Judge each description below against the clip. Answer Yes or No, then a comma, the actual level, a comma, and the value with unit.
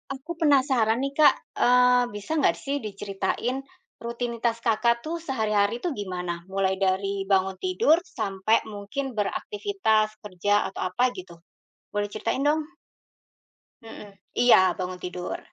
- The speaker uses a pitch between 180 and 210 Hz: No, high, 220 Hz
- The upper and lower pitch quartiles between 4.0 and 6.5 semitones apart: Yes, average, 4.9 semitones